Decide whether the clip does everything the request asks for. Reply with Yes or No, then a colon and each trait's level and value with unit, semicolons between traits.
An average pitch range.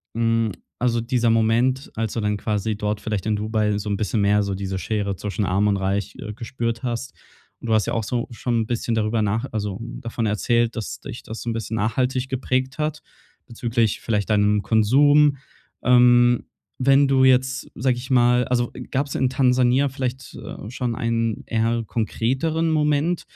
Yes: average, 3.1 semitones